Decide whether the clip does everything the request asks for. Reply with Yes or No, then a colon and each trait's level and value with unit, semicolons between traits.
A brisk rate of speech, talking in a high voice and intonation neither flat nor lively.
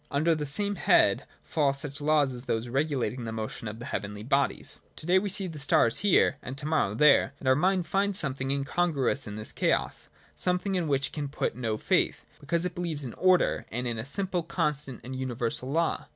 No: fast, 215 wpm; medium, 140 Hz; average, 5.0 semitones